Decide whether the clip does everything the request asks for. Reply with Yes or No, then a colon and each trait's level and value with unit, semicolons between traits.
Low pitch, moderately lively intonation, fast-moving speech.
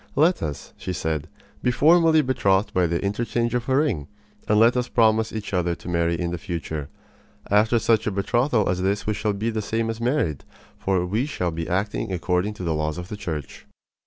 Yes: low, 100 Hz; average, 4.9 semitones; fast, 210 wpm